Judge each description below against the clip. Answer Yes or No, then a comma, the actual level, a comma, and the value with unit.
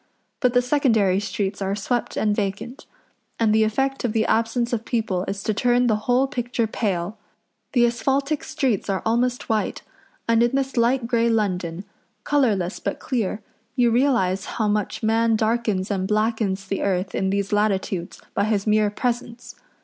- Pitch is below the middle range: No, high, 220 Hz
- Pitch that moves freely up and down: No, average, 3.4 semitones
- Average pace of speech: Yes, average, 165 wpm